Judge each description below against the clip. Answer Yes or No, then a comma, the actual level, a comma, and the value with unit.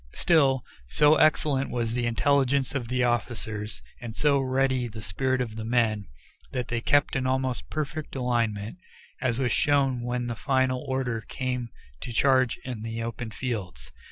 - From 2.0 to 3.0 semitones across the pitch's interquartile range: Yes, narrow, 2.5 semitones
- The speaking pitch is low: Yes, low, 125 Hz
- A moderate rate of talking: Yes, average, 160 wpm